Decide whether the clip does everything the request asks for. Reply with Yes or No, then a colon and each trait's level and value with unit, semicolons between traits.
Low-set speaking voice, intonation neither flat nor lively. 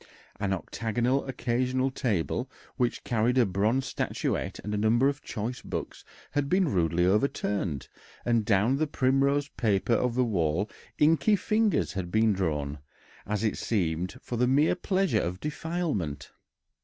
No: low, 115 Hz; wide, 5.9 semitones